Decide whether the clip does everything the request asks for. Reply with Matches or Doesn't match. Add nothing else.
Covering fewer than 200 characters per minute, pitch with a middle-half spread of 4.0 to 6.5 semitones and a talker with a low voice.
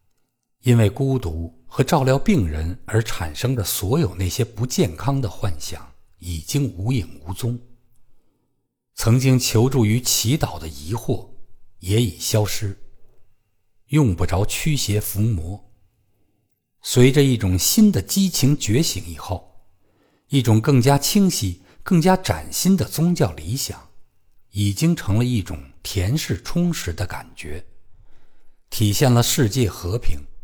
Matches